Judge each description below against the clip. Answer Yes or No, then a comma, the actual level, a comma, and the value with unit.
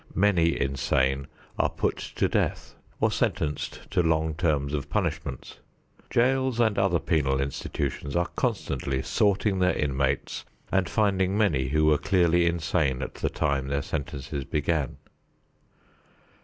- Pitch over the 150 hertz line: No, very low, 75 Hz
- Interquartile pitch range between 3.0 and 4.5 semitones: No, average, 5.0 semitones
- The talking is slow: Yes, slow, 130 wpm